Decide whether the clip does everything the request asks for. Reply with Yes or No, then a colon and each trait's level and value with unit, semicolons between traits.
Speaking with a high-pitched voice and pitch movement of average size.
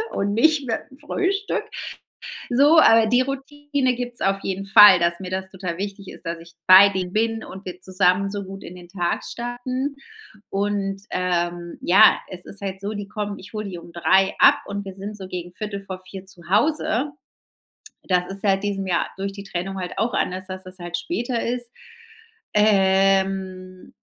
Yes: high, 195 Hz; average, 3.1 semitones